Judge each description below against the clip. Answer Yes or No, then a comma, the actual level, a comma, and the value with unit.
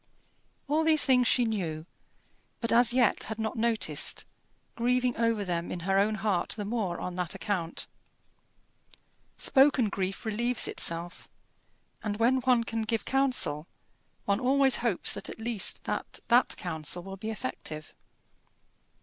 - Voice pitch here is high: Yes, high, 220 Hz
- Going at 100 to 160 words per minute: Yes, average, 140 wpm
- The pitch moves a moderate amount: Yes, average, 4.6 semitones